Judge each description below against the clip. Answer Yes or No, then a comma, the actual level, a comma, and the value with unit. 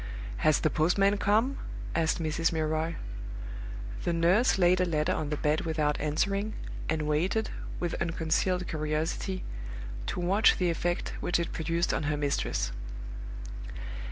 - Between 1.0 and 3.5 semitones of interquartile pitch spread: Yes, average, 2.9 semitones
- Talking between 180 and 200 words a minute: No, slow, 135 wpm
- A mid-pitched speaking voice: Yes, medium, 165 Hz